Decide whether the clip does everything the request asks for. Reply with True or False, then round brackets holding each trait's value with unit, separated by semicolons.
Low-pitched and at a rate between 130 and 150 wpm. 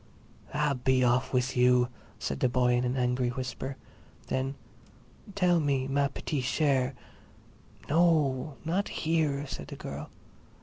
True (130 Hz; 135 wpm)